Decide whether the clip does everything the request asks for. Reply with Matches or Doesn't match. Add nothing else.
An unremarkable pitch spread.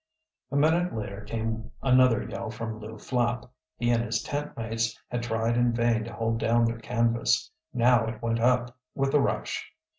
Doesn't match